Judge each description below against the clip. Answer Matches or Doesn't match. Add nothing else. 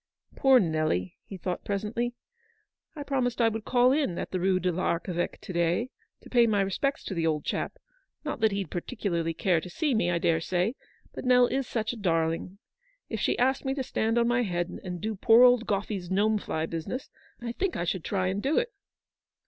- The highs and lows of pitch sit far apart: Matches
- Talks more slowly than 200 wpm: Doesn't match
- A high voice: Matches